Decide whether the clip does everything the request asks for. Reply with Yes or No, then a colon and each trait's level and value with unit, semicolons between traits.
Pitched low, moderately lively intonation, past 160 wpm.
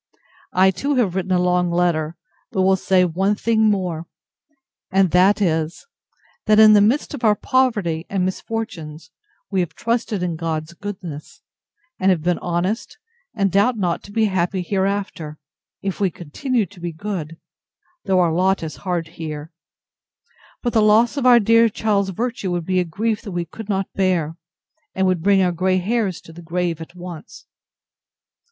No: medium, 185 Hz; average, 3.4 semitones; average, 170 wpm